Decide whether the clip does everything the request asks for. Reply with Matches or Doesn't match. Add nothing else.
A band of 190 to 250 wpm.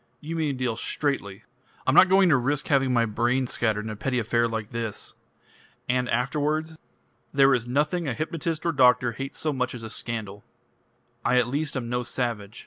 Matches